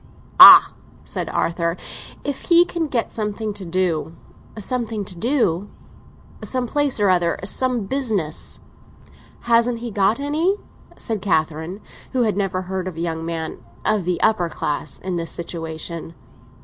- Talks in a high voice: Yes, high, 195 Hz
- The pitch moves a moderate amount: No, wide, 5.7 semitones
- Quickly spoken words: No, slow, 135 wpm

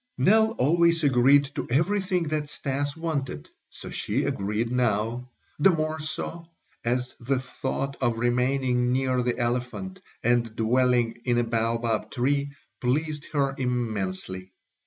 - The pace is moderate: No, slow, 130 wpm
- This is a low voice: Yes, low, 125 Hz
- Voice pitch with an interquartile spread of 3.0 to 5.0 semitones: Yes, average, 3.7 semitones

